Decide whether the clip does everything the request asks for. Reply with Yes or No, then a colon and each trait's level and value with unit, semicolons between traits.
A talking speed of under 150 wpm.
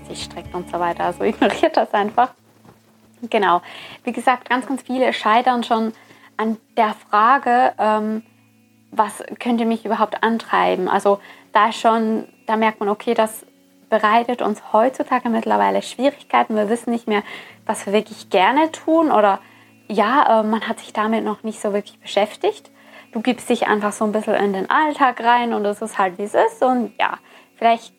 No: average, 175 wpm